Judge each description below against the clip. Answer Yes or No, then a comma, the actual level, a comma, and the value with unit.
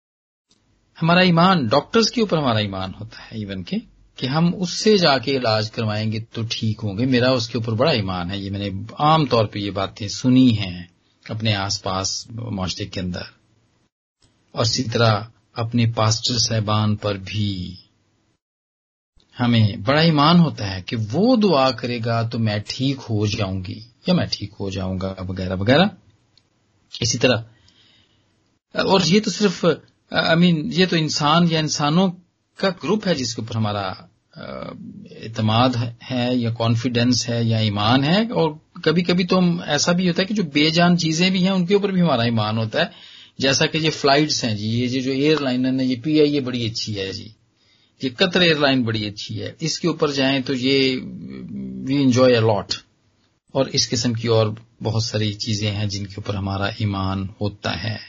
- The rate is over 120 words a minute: Yes, average, 170 wpm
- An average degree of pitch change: No, wide, 5.9 semitones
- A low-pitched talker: Yes, low, 115 Hz